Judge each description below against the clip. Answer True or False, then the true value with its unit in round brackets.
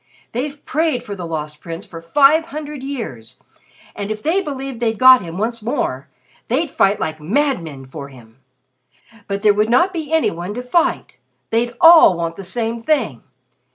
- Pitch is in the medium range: False (225 Hz)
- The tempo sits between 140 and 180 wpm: True (175 wpm)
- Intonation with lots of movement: True (8.8 semitones)